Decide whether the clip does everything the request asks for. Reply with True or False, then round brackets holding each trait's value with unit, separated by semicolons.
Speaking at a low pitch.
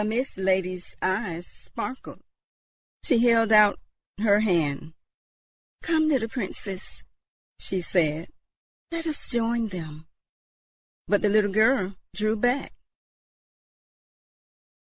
False (210 Hz)